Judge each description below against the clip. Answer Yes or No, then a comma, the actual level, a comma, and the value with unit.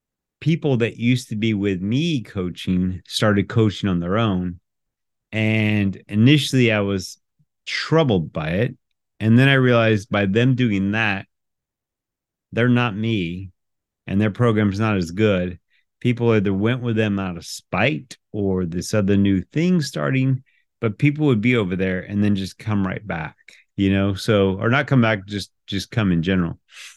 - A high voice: No, low, 105 Hz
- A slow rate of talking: No, average, 165 wpm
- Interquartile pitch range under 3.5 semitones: No, average, 3.8 semitones